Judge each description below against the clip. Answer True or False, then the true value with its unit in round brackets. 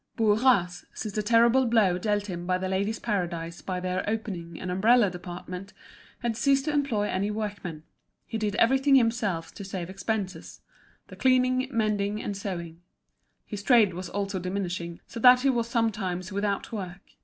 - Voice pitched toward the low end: False (205 Hz)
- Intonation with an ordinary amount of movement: True (3.9 semitones)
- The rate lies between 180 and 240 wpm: False (160 wpm)